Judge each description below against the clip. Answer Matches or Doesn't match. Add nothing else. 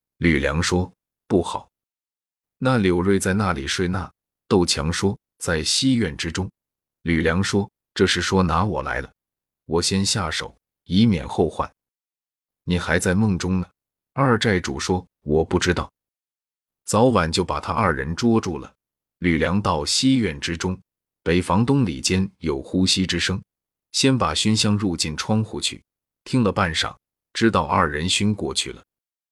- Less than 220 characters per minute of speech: Matches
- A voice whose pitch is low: Matches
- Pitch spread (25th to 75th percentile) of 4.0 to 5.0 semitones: Doesn't match